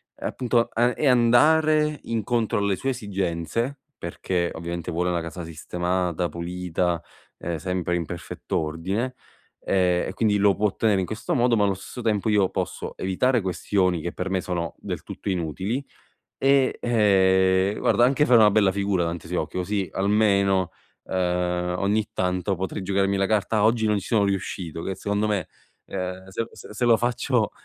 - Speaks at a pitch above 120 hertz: No, very low, 95 Hz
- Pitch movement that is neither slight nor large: Yes, average, 3.5 semitones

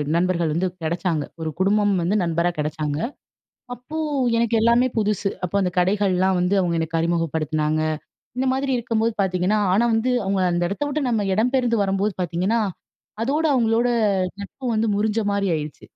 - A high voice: Yes, high, 195 Hz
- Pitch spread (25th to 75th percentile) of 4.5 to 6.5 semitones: Yes, average, 5.0 semitones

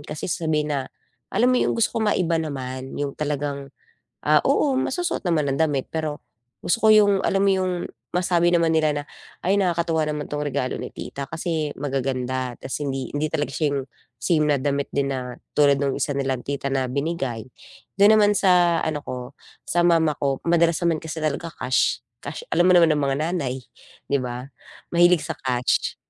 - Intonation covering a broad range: No, average, 3.8 semitones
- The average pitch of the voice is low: No, medium, 150 Hz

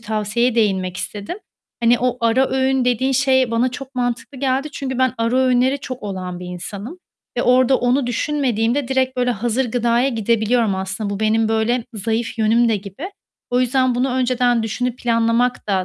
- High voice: Yes, high, 240 Hz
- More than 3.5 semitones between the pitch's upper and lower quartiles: No, average, 2.7 semitones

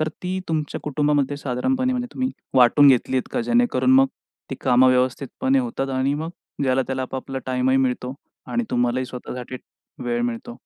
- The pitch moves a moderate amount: No, wide, 6.1 semitones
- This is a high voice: No, low, 135 Hz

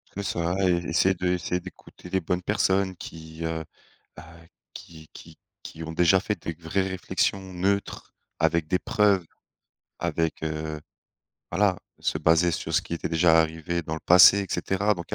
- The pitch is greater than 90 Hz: No, very low, 85 Hz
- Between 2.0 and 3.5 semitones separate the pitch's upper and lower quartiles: Yes, narrow, 2.6 semitones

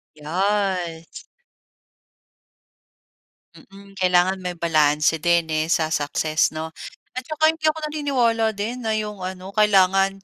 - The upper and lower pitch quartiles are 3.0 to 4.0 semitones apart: No, average, 4.5 semitones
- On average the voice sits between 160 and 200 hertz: Yes, high, 190 Hz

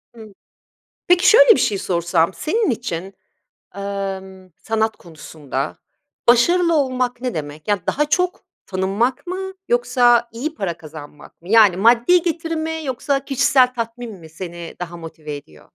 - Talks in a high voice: Yes, high, 225 Hz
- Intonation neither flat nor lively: No, wide, 7.9 semitones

